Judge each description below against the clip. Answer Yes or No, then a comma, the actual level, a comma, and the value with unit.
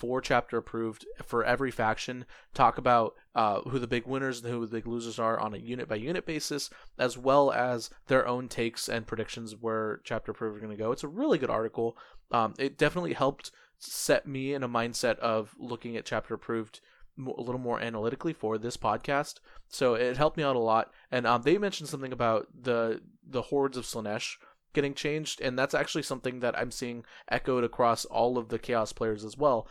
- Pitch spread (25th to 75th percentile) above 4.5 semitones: No, average, 2.8 semitones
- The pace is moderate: No, fast, 210 wpm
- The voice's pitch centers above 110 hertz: Yes, low, 120 Hz